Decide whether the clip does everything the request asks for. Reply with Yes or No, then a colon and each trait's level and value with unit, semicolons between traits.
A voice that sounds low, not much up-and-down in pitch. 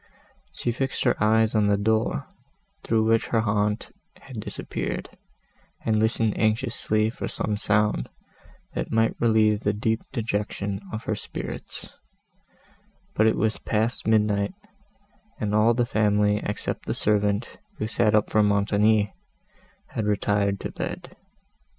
Yes: low, 110 Hz; narrow, 1.3 semitones